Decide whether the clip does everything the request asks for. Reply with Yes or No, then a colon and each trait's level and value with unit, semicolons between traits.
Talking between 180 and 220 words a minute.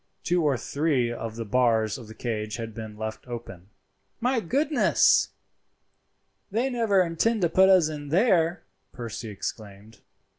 No: average, 145 wpm